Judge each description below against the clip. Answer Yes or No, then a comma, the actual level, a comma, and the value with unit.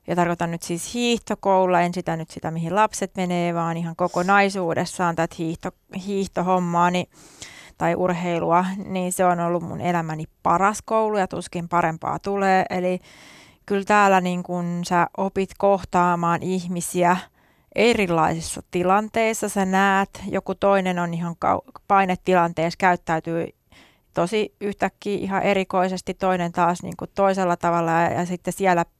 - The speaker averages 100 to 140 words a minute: Yes, average, 130 wpm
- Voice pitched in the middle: Yes, medium, 180 Hz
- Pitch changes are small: Yes, narrow, 2.1 semitones